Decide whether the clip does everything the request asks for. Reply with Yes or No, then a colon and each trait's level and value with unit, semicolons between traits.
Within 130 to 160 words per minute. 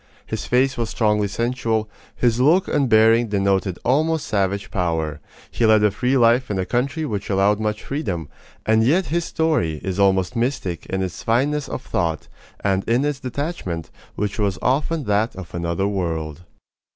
No: average, 170 wpm